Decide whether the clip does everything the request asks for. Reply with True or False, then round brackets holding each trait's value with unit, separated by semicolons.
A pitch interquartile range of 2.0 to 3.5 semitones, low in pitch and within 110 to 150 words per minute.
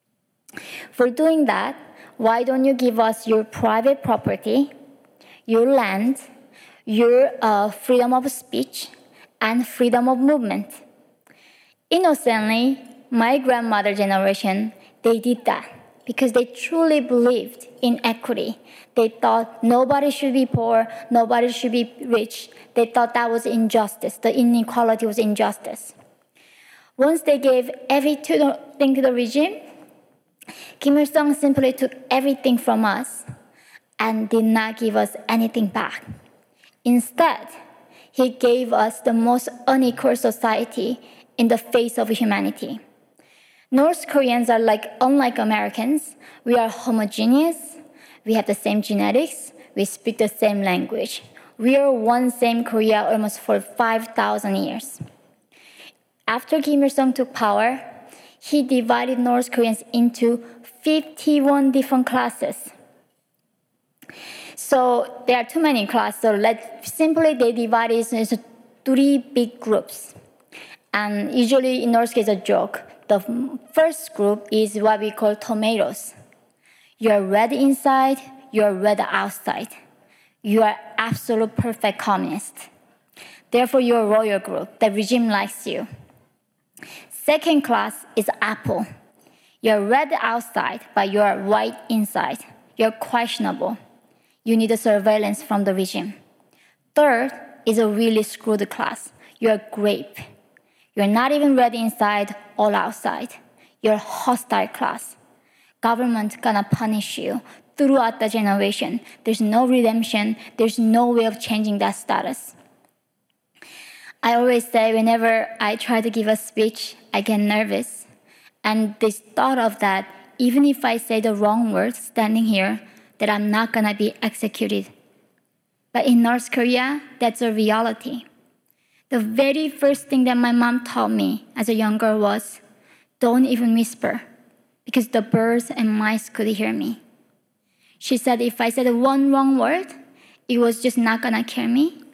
False (2.9 semitones; 235 Hz; 135 wpm)